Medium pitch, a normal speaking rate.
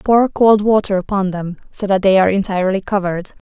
No: high, 195 Hz; average, 190 wpm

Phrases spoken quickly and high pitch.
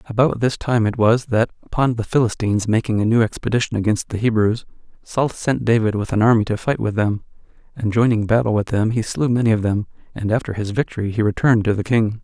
No: fast, 220 wpm; low, 110 Hz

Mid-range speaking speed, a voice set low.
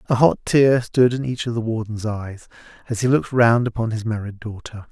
No: fast, 220 wpm; low, 115 Hz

